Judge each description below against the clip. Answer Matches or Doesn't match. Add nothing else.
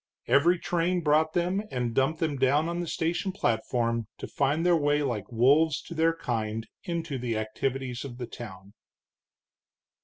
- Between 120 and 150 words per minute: Doesn't match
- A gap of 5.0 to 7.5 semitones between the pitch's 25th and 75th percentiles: Matches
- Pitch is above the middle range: Doesn't match